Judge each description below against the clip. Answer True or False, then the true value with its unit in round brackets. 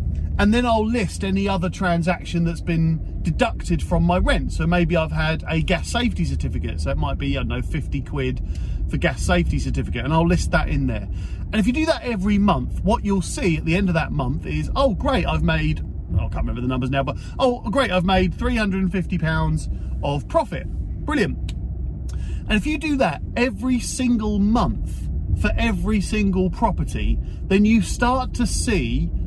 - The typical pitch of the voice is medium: True (160 Hz)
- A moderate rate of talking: True (195 wpm)